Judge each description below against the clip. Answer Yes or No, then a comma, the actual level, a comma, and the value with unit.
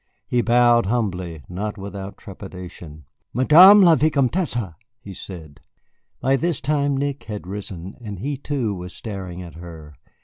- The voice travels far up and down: Yes, wide, 7.0 semitones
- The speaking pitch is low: Yes, low, 105 Hz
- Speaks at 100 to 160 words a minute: Yes, average, 140 wpm